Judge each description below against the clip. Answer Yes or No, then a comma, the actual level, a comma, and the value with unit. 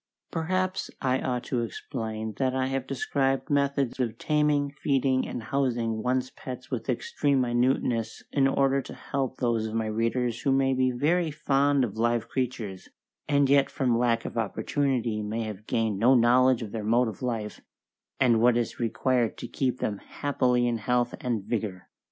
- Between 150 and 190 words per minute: Yes, average, 175 wpm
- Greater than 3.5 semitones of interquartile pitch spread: No, average, 2.9 semitones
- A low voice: Yes, low, 125 Hz